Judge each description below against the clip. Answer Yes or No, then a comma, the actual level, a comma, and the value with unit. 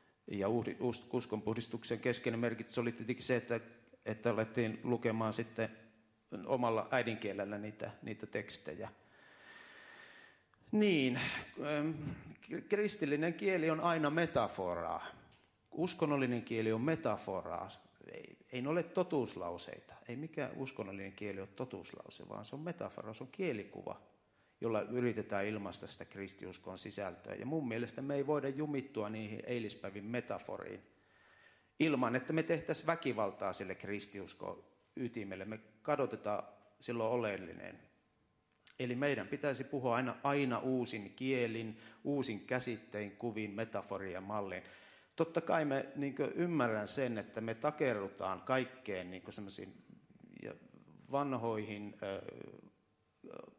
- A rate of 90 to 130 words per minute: Yes, average, 110 wpm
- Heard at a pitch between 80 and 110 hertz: No, low, 120 Hz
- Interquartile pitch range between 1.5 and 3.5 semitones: No, average, 4.8 semitones